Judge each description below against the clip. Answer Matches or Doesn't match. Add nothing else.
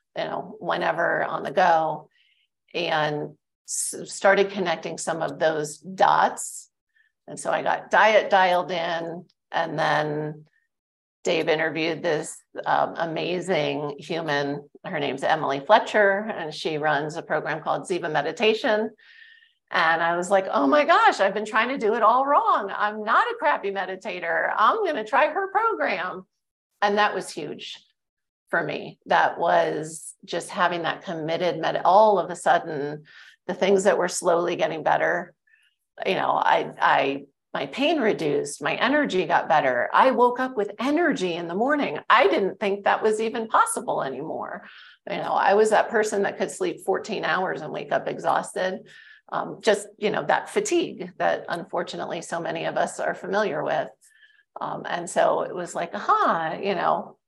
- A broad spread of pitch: Matches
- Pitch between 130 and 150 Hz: Doesn't match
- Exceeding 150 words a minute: Matches